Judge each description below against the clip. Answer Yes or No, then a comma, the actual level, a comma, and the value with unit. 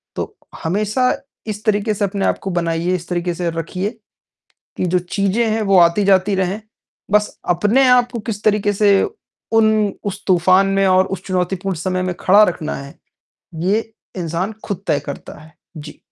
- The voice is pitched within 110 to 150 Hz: No, high, 190 Hz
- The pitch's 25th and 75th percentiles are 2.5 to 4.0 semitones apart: Yes, average, 2.9 semitones